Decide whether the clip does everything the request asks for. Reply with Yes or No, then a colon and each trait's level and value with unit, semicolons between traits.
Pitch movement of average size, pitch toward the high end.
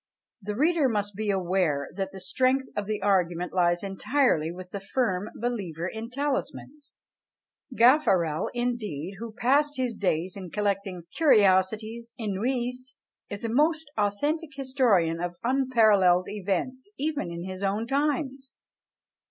No: wide, 5.7 semitones; high, 215 Hz